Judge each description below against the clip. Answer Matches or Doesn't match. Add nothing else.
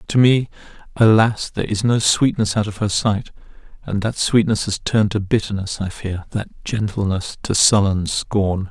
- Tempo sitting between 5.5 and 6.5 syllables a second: Doesn't match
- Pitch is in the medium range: Doesn't match